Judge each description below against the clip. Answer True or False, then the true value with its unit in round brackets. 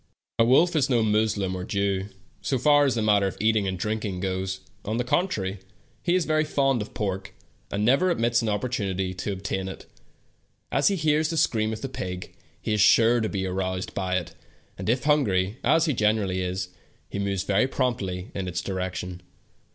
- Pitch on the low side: True (105 Hz)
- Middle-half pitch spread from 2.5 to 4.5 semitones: False (5.0 semitones)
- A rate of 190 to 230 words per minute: True (200 wpm)